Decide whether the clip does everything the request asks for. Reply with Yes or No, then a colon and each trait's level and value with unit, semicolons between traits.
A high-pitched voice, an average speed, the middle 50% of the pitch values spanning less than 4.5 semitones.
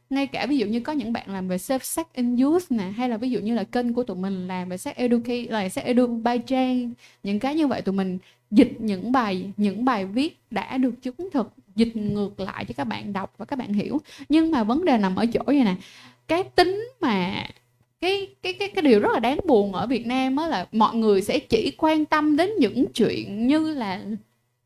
No: high, 245 Hz; average, 240 wpm; average, 5.3 semitones